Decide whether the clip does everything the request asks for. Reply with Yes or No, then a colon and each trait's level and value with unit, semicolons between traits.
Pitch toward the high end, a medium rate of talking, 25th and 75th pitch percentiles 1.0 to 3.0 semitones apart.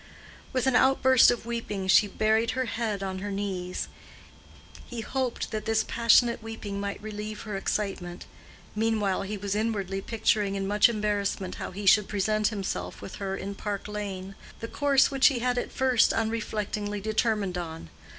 Yes: high, 210 Hz; average, 160 wpm; narrow, 2.4 semitones